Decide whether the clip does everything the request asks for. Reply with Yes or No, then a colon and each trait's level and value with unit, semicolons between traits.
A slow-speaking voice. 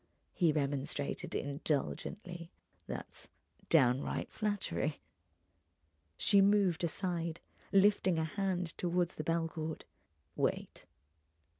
Yes: slow, 85 wpm